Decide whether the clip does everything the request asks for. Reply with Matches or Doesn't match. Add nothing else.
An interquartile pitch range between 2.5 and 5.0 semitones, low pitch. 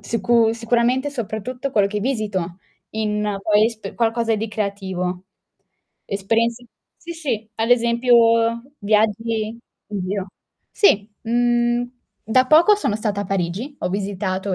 Doesn't match